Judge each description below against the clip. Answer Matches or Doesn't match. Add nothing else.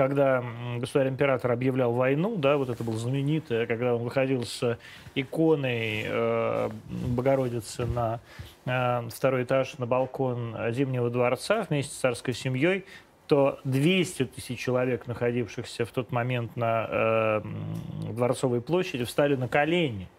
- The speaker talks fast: Doesn't match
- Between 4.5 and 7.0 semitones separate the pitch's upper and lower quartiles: Doesn't match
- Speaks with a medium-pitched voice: Doesn't match